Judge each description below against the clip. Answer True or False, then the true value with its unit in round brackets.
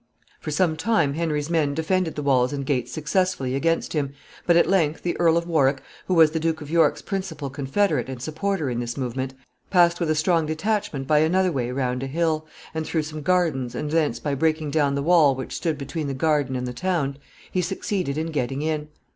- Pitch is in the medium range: True (155 Hz)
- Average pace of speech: False (215 wpm)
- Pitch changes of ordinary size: True (3.4 semitones)